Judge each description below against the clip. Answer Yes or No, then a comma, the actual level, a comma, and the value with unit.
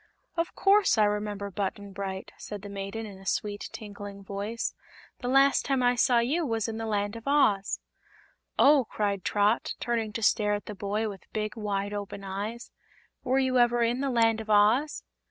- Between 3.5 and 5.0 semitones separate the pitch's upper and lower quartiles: No, average, 2.9 semitones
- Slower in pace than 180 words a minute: No, average, 190 wpm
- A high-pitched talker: Yes, high, 215 Hz